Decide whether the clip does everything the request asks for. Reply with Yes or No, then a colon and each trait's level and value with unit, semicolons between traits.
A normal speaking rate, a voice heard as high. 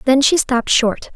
No: fast, 210 wpm; very high, 255 Hz